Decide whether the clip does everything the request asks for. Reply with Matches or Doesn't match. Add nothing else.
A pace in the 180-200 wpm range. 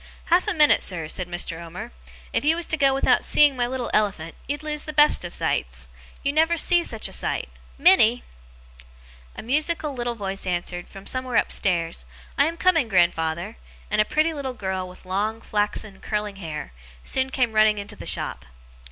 Matches